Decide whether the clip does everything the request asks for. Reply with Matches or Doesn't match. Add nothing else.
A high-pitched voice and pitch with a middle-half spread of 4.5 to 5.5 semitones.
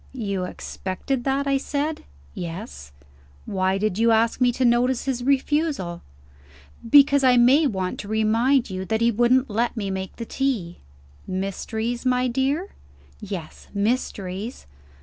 Matches